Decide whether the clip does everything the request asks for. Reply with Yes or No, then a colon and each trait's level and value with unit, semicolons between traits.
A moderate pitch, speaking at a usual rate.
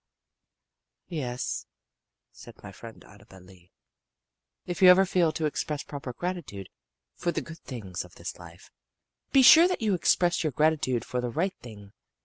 Yes: medium, 145 Hz; average, 155 wpm